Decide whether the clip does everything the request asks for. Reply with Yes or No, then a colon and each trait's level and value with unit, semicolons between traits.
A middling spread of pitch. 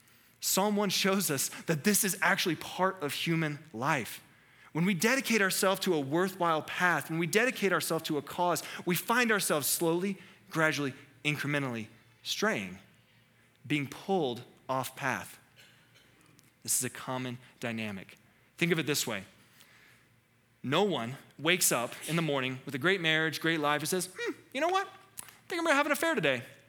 No: wide, 6.3 semitones